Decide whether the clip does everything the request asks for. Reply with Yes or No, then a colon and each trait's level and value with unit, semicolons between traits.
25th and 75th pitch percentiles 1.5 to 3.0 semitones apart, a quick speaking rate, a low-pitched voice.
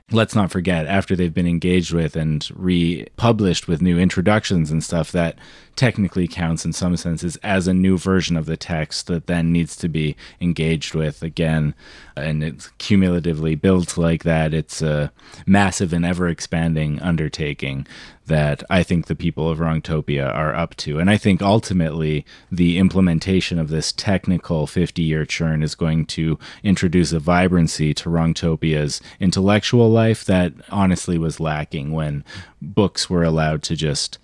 No: narrow, 2.6 semitones; average, 160 wpm; very low, 85 Hz